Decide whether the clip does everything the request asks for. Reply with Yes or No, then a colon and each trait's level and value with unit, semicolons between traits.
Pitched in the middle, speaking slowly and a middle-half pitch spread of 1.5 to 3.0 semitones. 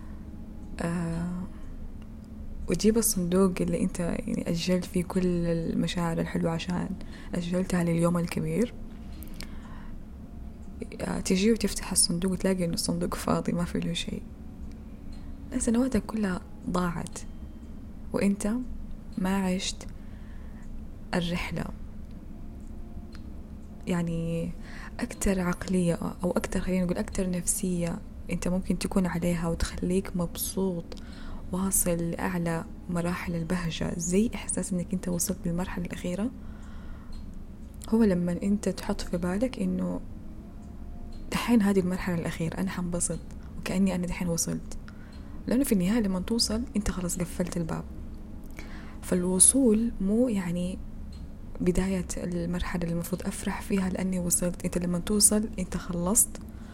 No: medium, 180 Hz; average, 110 wpm; narrow, 2.5 semitones